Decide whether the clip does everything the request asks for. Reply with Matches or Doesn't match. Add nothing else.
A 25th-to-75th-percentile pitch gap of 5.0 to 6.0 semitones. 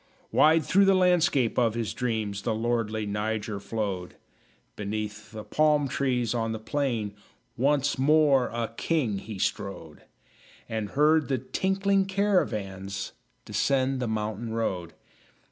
Matches